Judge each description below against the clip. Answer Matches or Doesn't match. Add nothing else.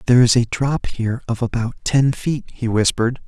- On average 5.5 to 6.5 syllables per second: Matches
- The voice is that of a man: Matches